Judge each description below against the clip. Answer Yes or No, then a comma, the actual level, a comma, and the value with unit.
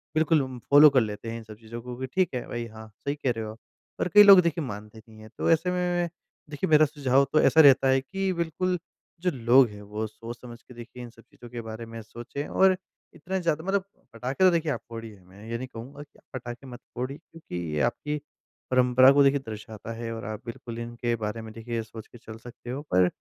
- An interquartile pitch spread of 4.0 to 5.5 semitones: Yes, average, 4.7 semitones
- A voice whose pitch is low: Yes, low, 125 Hz